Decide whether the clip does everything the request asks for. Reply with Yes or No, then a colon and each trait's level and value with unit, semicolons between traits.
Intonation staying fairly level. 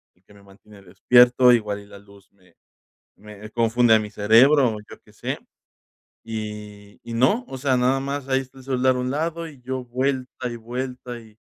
No: average, 3.7 semitones